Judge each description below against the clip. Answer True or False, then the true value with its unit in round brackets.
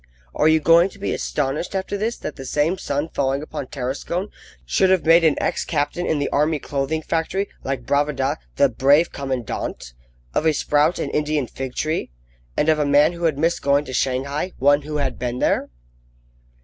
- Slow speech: False (195 wpm)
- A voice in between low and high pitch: True (150 Hz)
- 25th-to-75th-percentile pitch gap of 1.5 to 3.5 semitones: True (2.9 semitones)